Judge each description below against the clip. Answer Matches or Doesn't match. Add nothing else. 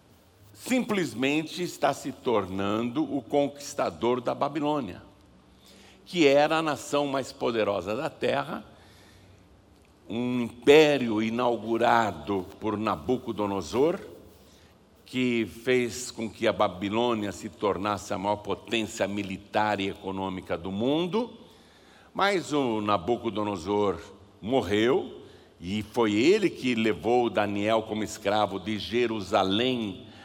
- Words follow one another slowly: Matches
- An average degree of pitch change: Matches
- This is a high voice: Doesn't match